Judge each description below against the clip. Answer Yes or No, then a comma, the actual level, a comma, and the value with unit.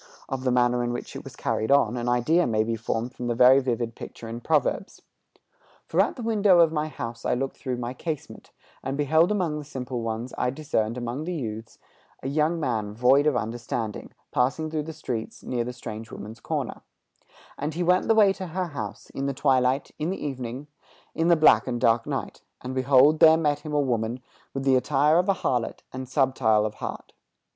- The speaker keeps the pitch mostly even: No, average, 4.3 semitones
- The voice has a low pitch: Yes, low, 130 Hz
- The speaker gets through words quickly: Yes, fast, 210 wpm